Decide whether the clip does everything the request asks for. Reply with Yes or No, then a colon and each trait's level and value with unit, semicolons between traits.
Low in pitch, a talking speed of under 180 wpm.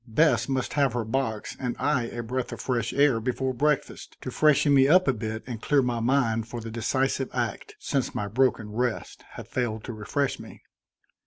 No: low, 125 Hz; average, 195 wpm